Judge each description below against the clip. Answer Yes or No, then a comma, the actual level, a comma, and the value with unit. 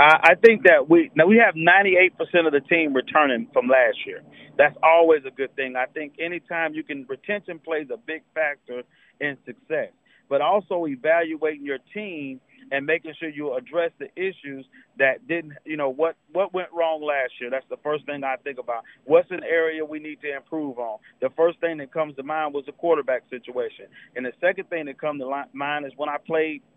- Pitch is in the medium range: Yes, medium, 155 Hz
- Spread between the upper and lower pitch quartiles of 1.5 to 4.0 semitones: Yes, average, 3.2 semitones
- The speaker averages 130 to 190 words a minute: No, fast, 205 wpm